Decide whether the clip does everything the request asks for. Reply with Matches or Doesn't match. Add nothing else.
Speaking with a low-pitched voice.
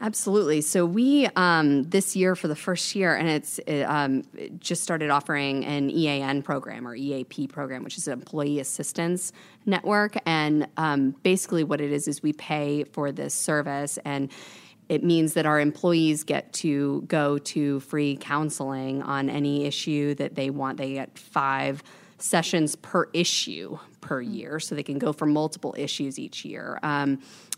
Doesn't match